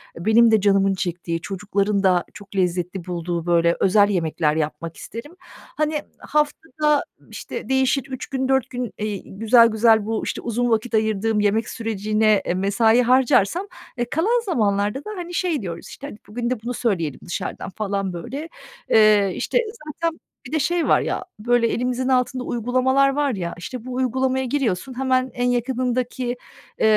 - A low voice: No, high, 230 Hz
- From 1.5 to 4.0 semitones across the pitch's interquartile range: No, average, 4.7 semitones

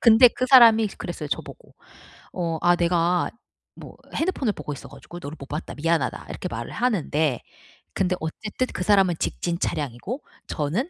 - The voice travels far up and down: Yes, wide, 6.3 semitones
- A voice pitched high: No, medium, 175 Hz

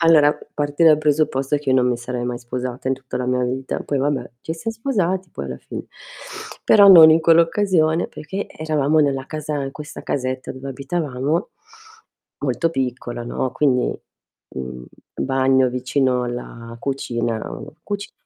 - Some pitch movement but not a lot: Yes, average, 3.9 semitones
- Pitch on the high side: No, low, 135 Hz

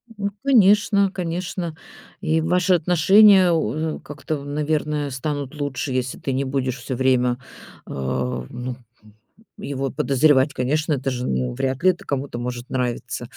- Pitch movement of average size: Yes, average, 4.3 semitones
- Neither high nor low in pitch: Yes, medium, 145 Hz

